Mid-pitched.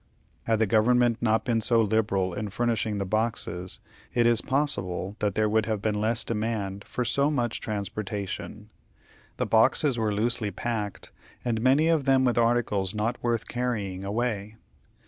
No: low, 110 Hz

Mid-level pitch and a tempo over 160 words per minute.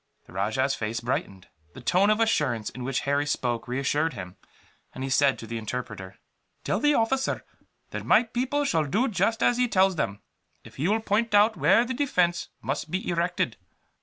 Yes: medium, 160 Hz; average, 190 wpm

